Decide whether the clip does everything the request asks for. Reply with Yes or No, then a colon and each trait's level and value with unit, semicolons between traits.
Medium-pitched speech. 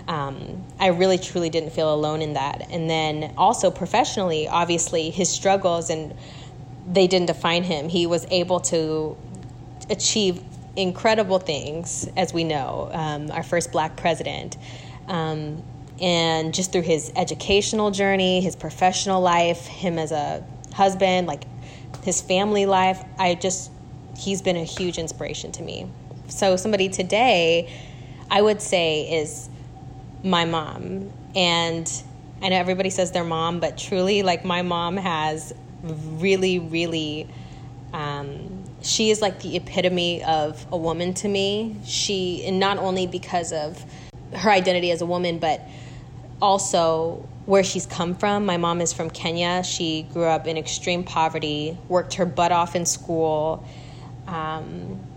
Yes: medium, 170 Hz